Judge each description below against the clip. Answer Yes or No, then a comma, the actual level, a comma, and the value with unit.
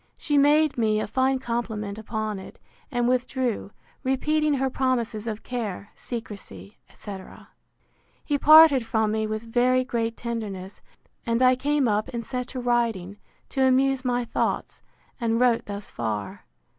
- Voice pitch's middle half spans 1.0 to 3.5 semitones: Yes, average, 3.2 semitones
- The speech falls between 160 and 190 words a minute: No, average, 145 wpm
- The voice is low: No, high, 235 Hz